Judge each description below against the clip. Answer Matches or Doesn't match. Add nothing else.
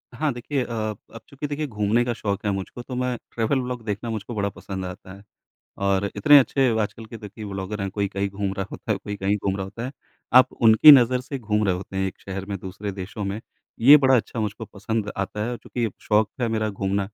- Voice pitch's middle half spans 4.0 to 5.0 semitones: Doesn't match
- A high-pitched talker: Doesn't match